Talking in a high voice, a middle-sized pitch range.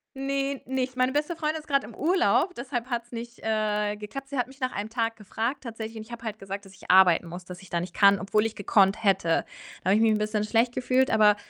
Yes: high, 225 Hz; average, 4.0 semitones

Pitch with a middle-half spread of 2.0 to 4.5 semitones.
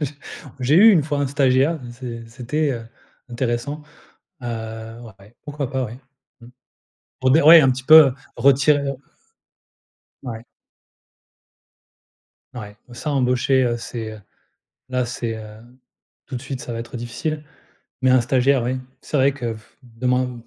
Yes: average, 2.9 semitones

